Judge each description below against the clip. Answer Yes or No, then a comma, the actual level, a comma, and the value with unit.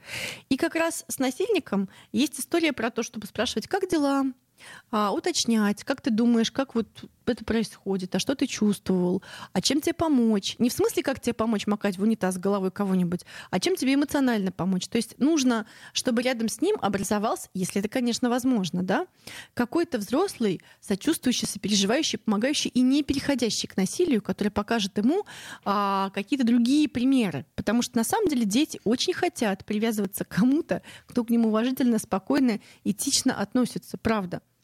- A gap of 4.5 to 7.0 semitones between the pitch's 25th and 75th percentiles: Yes, average, 5.1 semitones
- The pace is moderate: No, fast, 165 wpm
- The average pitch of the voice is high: Yes, high, 230 Hz